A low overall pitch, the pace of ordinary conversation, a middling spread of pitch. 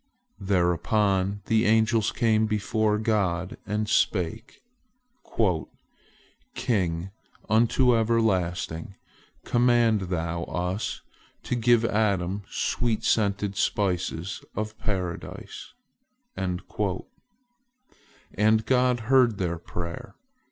No: low, 105 Hz; slow, 80 wpm; average, 3.6 semitones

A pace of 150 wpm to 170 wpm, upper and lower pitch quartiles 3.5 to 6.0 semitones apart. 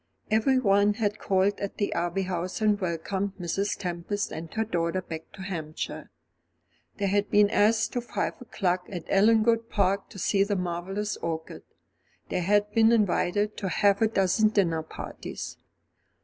No: average, 155 wpm; average, 2.8 semitones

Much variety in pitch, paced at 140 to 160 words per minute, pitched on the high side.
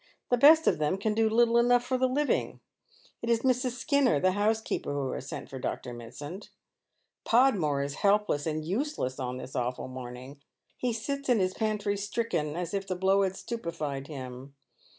No: wide, 8.7 semitones; average, 185 wpm; high, 195 Hz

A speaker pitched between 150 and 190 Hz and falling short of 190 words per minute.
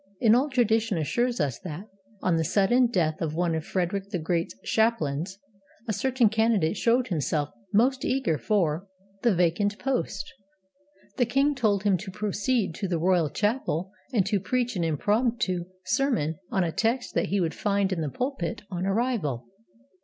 No: high, 200 Hz; average, 170 wpm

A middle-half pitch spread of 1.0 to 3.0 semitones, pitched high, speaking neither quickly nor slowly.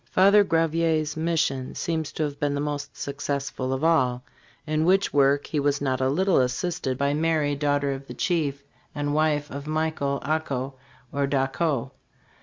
No: narrow, 2.4 semitones; medium, 145 Hz; average, 170 wpm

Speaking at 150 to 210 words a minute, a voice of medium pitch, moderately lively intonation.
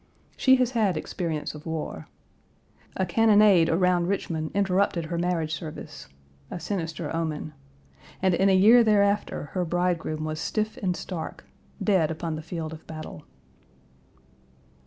No: slow, 135 wpm; medium, 175 Hz; average, 3.7 semitones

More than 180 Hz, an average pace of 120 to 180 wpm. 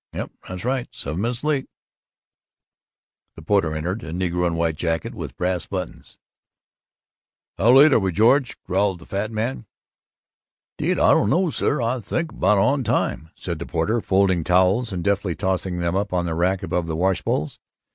No: very low, 95 Hz; average, 175 wpm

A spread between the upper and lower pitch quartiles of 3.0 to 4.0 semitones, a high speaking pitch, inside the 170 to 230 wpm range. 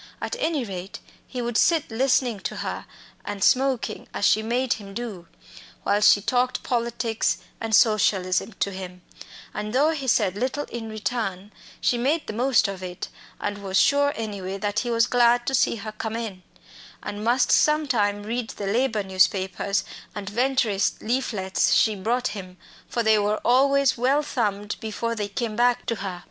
Yes: average, 3.4 semitones; high, 220 Hz; average, 175 wpm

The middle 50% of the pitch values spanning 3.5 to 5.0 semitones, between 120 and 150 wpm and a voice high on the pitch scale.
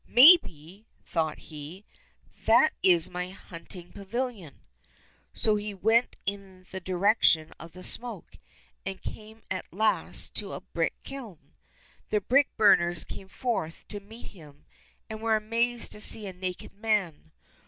Yes: average, 4.1 semitones; average, 145 wpm; high, 200 Hz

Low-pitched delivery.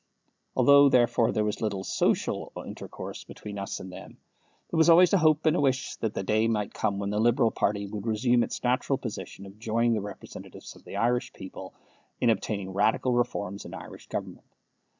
Yes: low, 110 Hz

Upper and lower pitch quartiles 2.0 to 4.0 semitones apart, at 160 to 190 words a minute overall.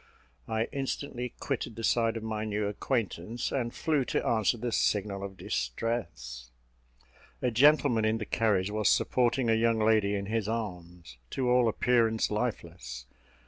No: average, 3.1 semitones; average, 150 wpm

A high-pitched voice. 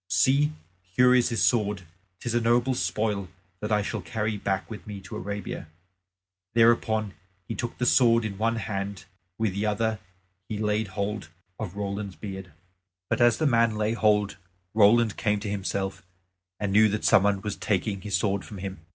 No: low, 105 Hz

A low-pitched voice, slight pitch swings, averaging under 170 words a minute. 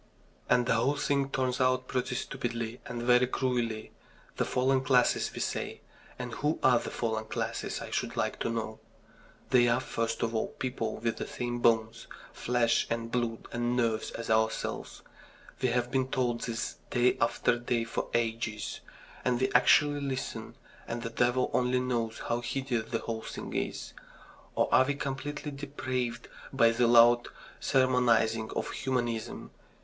Yes: low, 120 Hz; narrow, 1.8 semitones; average, 160 wpm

